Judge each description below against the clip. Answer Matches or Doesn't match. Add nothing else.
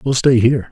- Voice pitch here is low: Matches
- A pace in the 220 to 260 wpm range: Matches